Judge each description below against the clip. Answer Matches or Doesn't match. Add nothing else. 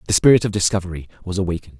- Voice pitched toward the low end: Matches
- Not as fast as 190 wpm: Doesn't match